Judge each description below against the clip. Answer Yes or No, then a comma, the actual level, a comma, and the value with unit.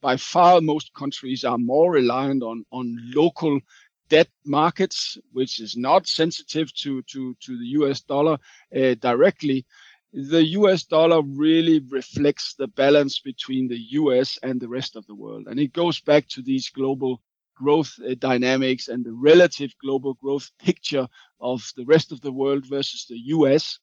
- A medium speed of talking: Yes, average, 165 wpm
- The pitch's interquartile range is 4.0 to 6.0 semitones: No, average, 3.2 semitones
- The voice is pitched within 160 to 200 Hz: No, low, 135 Hz